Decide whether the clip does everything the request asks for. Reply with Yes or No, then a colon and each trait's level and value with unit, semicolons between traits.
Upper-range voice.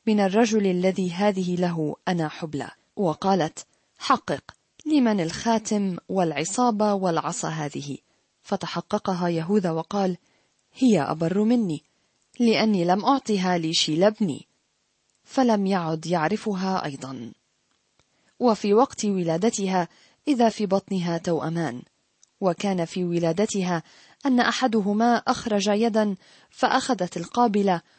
Yes: high, 195 Hz